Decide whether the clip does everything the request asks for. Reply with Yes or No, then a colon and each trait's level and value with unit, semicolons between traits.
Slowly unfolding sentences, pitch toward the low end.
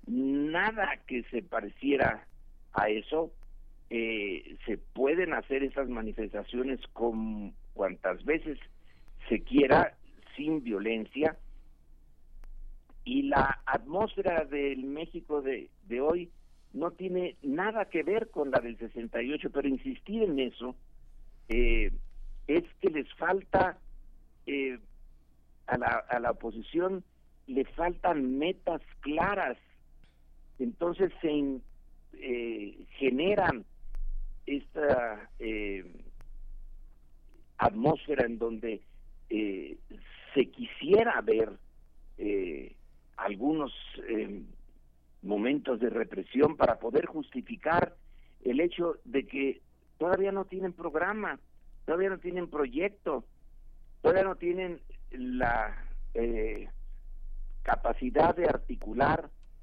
Yes: slow, 100 wpm; low, 120 Hz